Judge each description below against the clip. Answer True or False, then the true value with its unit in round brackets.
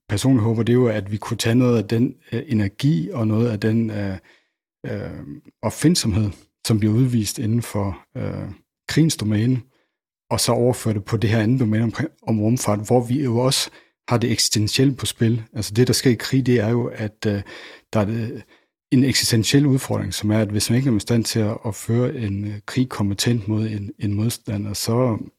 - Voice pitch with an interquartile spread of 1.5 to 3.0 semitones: True (2.6 semitones)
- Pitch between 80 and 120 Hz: True (115 Hz)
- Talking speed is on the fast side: False (210 wpm)